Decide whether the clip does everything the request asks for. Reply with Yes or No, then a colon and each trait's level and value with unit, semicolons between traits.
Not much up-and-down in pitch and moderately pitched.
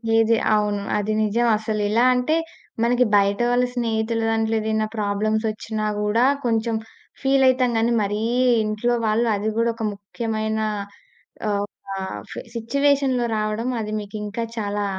No: narrow, 2.0 semitones; high, 220 Hz